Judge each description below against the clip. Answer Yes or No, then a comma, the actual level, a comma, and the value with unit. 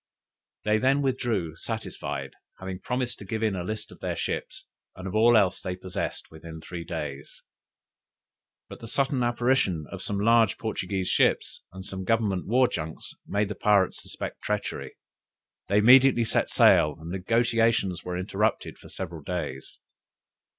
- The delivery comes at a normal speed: Yes, average, 155 wpm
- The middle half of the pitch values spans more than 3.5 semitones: Yes, average, 4.2 semitones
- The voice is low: Yes, low, 100 Hz